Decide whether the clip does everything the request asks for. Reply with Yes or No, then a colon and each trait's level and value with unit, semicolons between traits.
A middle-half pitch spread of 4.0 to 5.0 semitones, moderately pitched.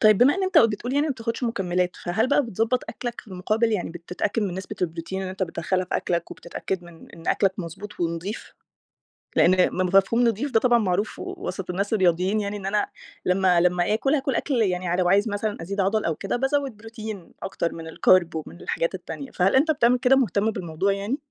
No: average, 4.3 semitones; high, 200 Hz